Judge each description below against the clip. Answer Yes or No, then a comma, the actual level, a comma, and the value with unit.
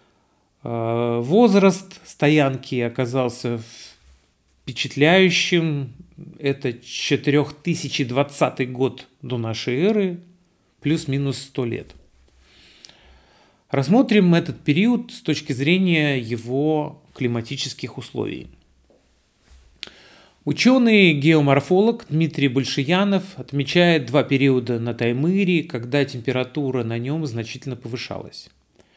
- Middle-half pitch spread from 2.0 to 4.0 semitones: No, average, 5.0 semitones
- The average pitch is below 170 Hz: Yes, medium, 140 Hz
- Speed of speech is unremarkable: No, slow, 75 wpm